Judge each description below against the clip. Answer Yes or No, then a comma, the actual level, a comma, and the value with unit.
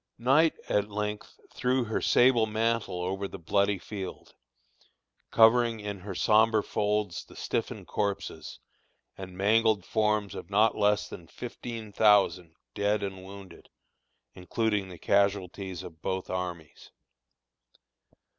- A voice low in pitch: Yes, low, 105 Hz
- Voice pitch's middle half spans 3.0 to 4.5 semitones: No, narrow, 2.6 semitones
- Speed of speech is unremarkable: No, slow, 120 wpm